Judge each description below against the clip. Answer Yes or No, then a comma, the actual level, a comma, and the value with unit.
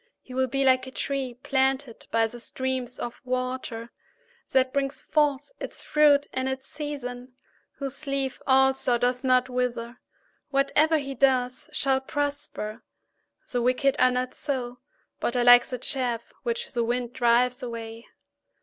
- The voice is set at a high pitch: Yes, very high, 255 Hz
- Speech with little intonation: Yes, narrow, 1.8 semitones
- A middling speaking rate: Yes, average, 150 wpm